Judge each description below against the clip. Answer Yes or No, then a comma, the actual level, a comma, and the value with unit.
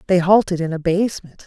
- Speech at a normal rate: Yes, average, 165 wpm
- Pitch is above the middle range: No, medium, 180 Hz